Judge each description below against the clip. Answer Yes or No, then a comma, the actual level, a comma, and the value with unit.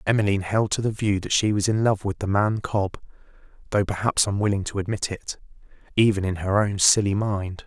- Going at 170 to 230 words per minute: Yes, fast, 205 wpm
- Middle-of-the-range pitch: No, low, 100 Hz